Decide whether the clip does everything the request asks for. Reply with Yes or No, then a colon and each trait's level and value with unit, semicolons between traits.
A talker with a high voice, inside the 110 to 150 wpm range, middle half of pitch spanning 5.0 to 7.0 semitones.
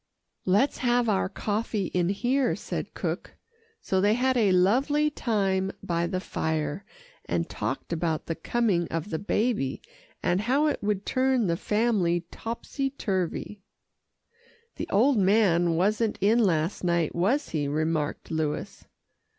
Yes: high, 195 Hz; average, 140 wpm; wide, 5.6 semitones